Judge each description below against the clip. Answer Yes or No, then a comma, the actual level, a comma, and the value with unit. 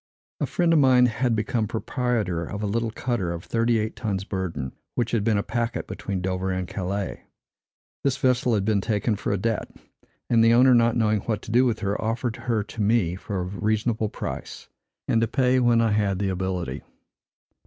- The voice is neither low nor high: No, low, 110 Hz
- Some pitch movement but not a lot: Yes, average, 3.2 semitones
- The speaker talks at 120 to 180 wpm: No, average, 200 wpm